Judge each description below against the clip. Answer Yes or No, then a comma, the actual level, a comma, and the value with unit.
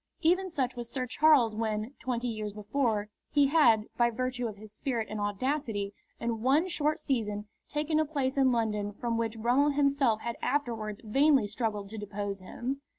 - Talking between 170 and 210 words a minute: Yes, average, 175 wpm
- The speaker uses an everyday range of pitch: Yes, average, 4.6 semitones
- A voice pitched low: No, high, 235 Hz